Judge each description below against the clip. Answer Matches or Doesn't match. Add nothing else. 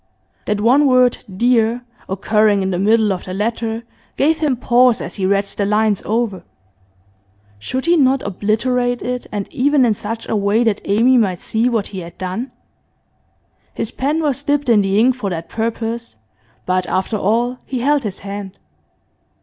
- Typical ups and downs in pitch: Matches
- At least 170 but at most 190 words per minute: Matches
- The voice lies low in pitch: Doesn't match